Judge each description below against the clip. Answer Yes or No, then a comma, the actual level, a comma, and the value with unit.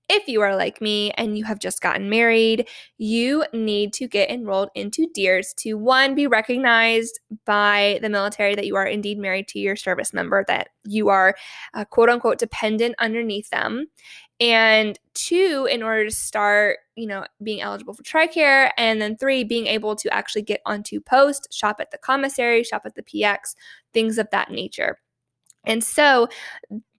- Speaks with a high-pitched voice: Yes, high, 220 Hz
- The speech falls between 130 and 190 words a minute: Yes, average, 175 wpm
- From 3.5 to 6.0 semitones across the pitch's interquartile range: No, average, 2.9 semitones